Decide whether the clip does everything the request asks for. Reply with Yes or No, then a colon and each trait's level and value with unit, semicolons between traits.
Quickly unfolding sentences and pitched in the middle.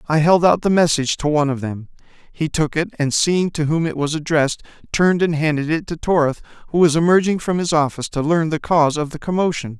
Yes: fast, 235 wpm; medium, 155 Hz